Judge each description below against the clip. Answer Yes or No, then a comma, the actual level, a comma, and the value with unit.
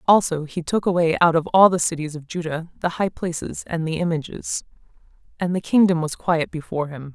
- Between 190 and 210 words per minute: Yes, average, 200 wpm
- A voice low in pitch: No, medium, 165 Hz